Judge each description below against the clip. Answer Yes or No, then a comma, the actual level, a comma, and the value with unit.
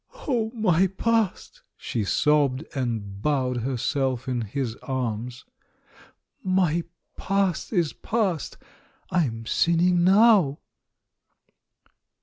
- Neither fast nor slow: No, slow, 95 wpm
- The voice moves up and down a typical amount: No, wide, 6.8 semitones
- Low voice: No, medium, 150 Hz